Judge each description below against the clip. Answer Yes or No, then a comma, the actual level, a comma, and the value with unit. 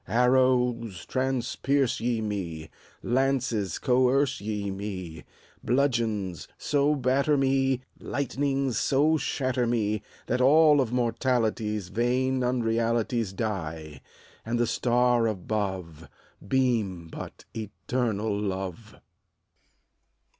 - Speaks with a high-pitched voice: No, low, 120 Hz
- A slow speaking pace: Yes, slow, 90 wpm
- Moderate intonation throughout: Yes, average, 4.0 semitones